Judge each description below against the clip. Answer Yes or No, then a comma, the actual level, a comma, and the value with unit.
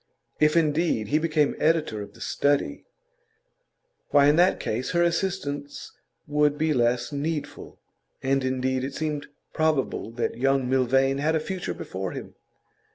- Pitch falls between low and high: Yes, medium, 145 Hz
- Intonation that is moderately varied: Yes, average, 3.3 semitones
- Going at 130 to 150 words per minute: Yes, average, 145 wpm